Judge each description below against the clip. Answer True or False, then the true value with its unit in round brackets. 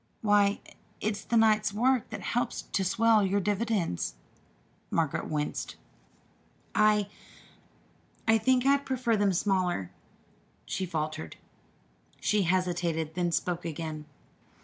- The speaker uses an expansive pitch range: False (4.6 semitones)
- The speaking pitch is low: False (200 Hz)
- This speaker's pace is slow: True (110 wpm)